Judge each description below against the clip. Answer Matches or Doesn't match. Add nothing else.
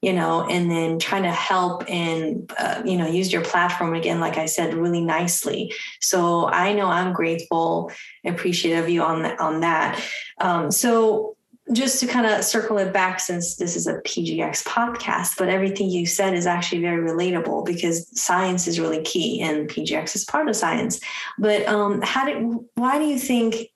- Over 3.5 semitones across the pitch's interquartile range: Matches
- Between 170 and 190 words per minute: Matches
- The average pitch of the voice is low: Doesn't match